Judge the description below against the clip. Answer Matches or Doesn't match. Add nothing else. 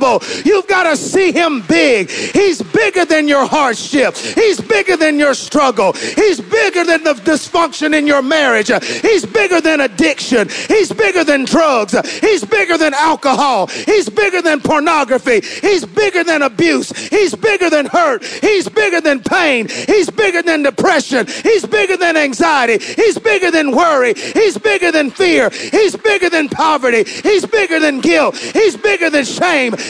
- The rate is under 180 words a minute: Matches